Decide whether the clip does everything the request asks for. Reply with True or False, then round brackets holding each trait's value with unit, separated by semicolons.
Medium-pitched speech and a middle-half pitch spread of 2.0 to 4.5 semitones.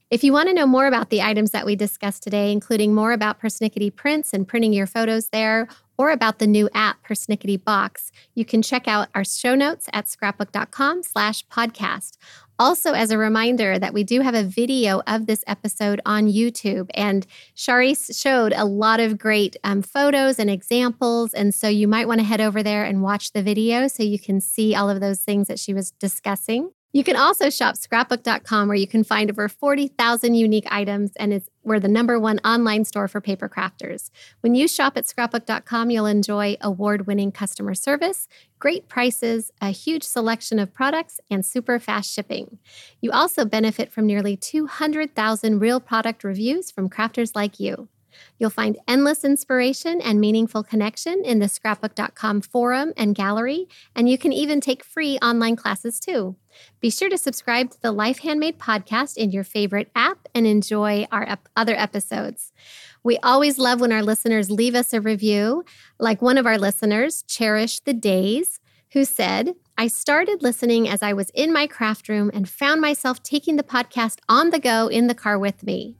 False (225 Hz; 3.4 semitones)